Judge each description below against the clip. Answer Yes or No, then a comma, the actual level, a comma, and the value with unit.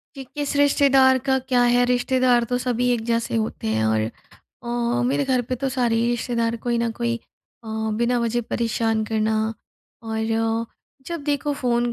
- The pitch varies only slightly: Yes, narrow, 1.9 semitones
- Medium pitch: No, high, 240 Hz